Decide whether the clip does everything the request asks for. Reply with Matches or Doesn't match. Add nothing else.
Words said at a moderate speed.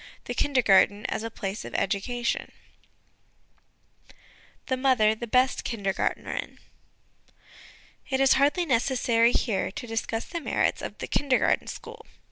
Doesn't match